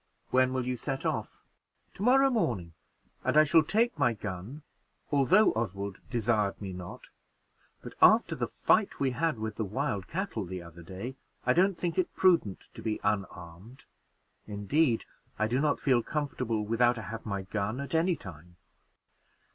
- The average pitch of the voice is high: No, low, 120 Hz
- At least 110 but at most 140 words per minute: No, average, 165 wpm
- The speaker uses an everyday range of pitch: No, wide, 6.9 semitones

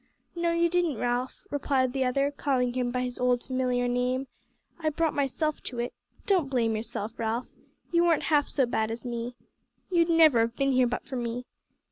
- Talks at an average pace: Yes, average, 190 wpm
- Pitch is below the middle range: No, very high, 255 Hz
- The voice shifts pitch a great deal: No, average, 3.1 semitones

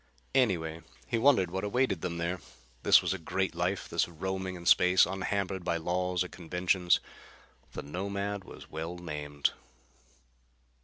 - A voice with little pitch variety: Yes, narrow, 2.0 semitones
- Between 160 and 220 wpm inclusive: No, average, 145 wpm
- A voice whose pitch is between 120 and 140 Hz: No, very low, 90 Hz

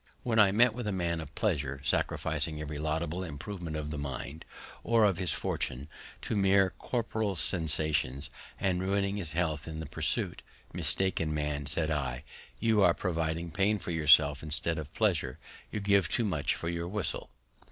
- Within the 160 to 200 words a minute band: Yes, average, 170 wpm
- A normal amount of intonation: Yes, average, 4.4 semitones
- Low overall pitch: Yes, very low, 85 Hz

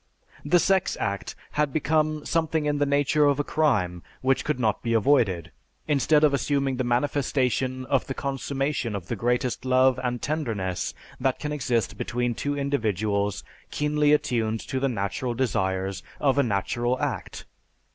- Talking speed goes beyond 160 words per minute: No, average, 155 wpm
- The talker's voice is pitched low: Yes, low, 130 Hz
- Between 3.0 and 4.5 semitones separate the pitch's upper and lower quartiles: Yes, average, 4.2 semitones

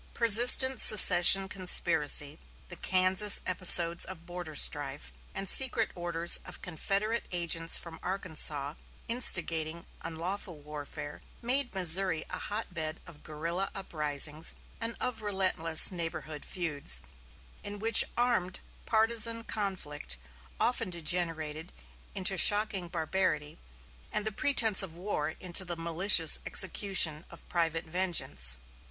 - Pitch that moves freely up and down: No, average, 3.9 semitones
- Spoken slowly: Yes, slow, 110 wpm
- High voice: No, medium, 180 Hz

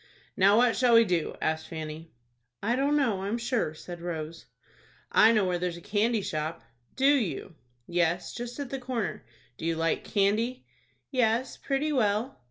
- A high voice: Yes, high, 210 Hz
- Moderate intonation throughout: No, wide, 6.2 semitones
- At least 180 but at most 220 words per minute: No, average, 170 wpm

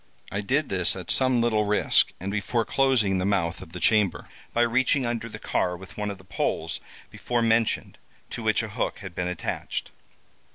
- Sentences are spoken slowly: No, average, 195 wpm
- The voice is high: No, low, 105 Hz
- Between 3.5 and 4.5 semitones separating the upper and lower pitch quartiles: Yes, average, 3.9 semitones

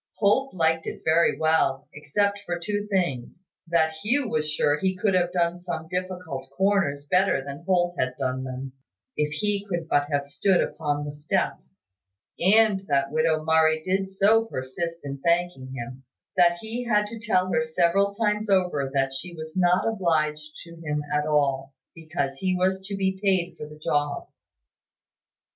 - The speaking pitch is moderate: Yes, medium, 170 Hz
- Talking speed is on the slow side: No, average, 170 wpm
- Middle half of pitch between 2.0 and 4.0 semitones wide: No, average, 4.5 semitones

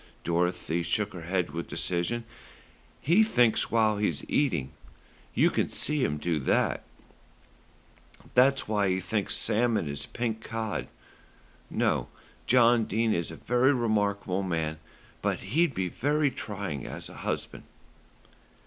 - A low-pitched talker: Yes, low, 105 Hz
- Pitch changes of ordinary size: No, wide, 5.8 semitones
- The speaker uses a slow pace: Yes, slow, 130 wpm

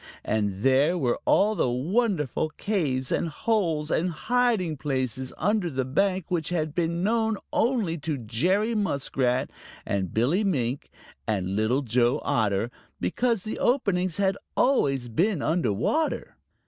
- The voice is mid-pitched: Yes, medium, 160 Hz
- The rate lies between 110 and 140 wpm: Yes, slow, 135 wpm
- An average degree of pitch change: No, wide, 7.7 semitones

